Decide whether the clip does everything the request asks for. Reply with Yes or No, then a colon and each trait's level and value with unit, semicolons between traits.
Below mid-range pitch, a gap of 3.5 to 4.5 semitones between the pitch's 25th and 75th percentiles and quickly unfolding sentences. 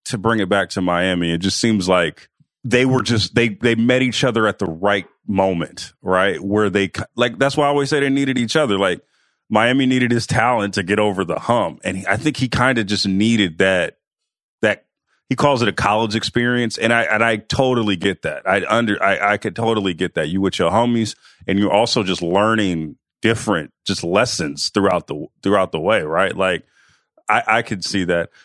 Yes: low, 110 Hz; average, 3.8 semitones; fast, 215 wpm